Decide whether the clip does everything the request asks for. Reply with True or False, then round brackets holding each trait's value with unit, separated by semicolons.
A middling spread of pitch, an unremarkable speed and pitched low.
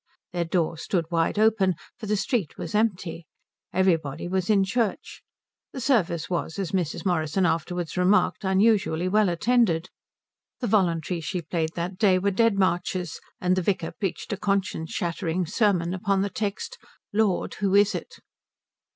False (3.1 semitones; 155 wpm; 185 Hz)